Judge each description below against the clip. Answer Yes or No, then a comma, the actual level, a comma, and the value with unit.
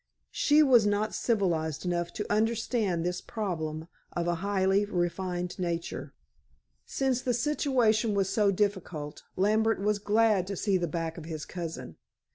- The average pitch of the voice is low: No, high, 195 Hz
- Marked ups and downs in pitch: No, average, 3.9 semitones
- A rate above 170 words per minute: No, average, 145 wpm